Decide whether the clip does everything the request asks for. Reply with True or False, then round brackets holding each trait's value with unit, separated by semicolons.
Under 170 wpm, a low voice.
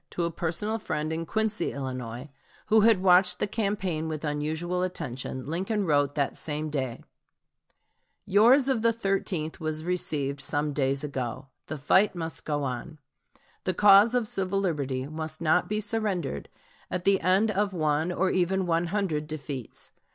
False (160 wpm; 165 Hz)